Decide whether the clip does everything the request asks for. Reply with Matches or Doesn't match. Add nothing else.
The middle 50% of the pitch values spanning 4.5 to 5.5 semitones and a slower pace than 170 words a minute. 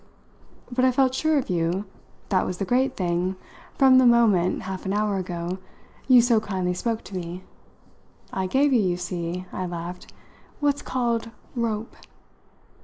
Matches